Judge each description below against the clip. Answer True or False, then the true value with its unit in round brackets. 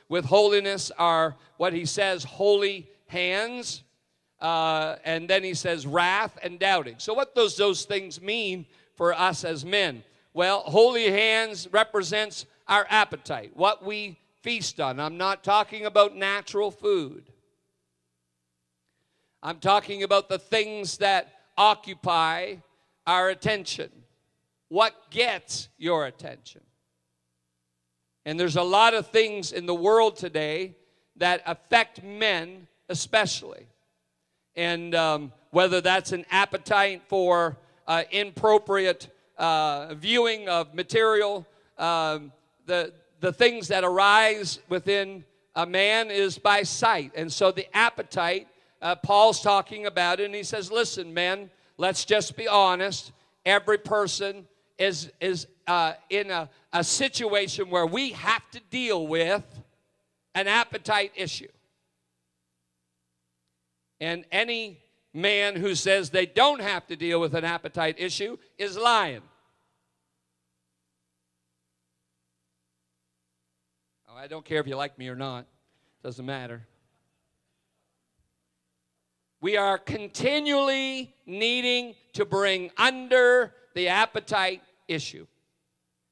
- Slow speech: True (120 wpm)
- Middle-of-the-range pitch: True (180 Hz)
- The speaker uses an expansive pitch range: True (5.8 semitones)